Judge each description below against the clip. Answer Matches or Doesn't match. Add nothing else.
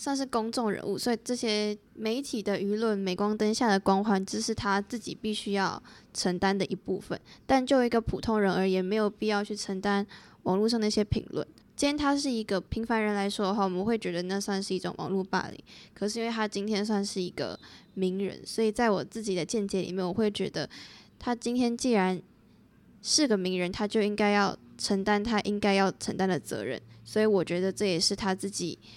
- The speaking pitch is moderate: Doesn't match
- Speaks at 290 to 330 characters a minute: Matches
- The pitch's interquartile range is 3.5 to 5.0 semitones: Doesn't match